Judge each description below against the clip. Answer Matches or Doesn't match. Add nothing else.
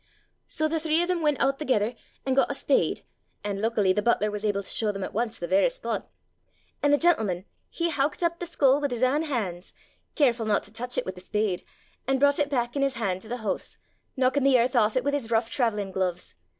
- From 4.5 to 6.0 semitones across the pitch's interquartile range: Matches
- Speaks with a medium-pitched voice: Doesn't match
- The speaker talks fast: Matches